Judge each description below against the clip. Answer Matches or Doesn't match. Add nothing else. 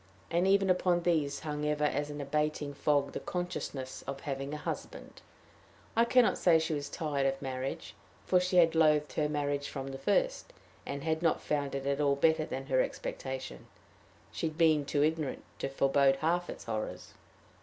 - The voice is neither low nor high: Matches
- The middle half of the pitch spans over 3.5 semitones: Doesn't match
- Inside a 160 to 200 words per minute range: Matches